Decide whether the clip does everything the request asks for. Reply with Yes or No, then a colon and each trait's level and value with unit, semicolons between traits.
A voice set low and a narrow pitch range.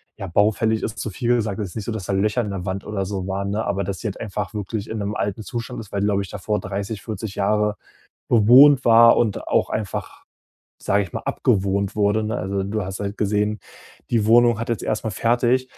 Yes: low, 105 Hz; narrow, 2.2 semitones